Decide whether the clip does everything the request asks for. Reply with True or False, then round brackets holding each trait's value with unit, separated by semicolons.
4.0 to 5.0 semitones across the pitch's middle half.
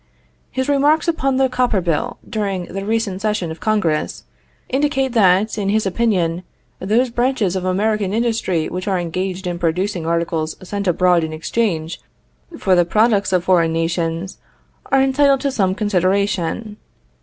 True (4.6 semitones)